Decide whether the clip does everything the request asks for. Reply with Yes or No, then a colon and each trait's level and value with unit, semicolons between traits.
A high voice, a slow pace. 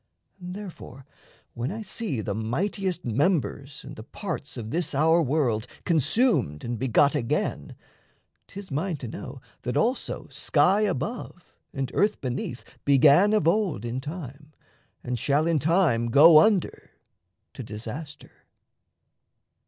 No: medium, 150 Hz; slow, 130 wpm